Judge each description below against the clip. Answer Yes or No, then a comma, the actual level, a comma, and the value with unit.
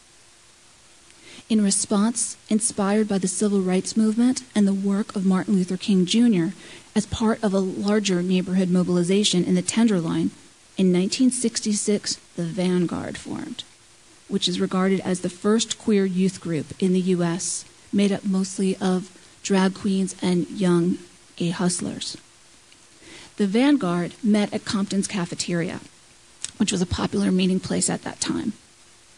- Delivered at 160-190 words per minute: No, average, 140 wpm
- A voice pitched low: No, high, 190 Hz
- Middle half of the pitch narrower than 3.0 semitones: Yes, narrow, 2.6 semitones